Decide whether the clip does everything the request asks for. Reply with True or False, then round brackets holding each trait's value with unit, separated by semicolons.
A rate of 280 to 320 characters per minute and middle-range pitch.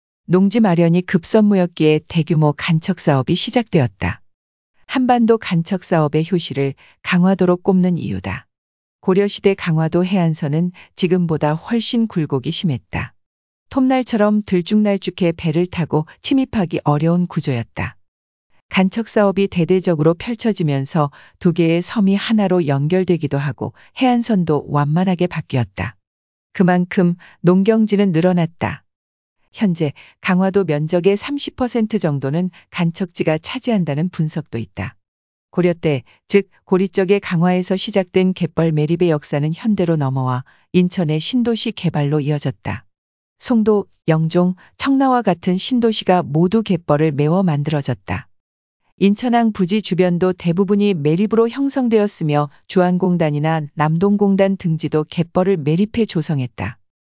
True (295 characters per minute; 175 Hz)